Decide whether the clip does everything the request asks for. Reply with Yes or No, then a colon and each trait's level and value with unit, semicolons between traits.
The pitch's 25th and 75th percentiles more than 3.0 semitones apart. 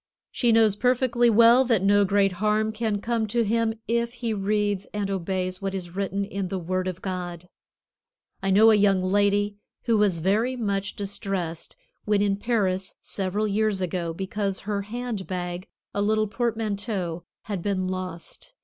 No: narrow, 2.6 semitones